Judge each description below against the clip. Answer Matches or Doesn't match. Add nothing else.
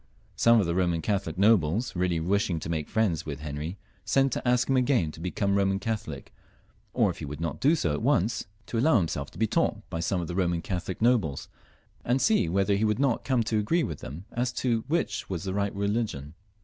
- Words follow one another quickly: Matches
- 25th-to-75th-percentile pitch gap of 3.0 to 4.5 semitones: Doesn't match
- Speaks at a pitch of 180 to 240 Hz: Doesn't match